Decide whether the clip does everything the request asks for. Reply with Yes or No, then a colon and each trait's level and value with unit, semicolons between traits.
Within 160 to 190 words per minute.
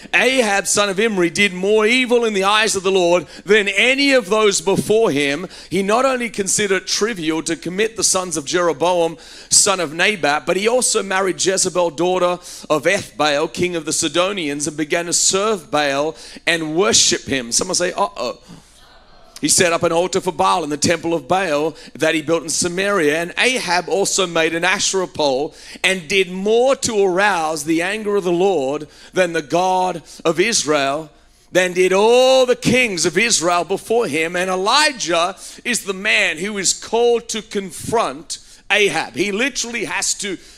Yes: average, 180 wpm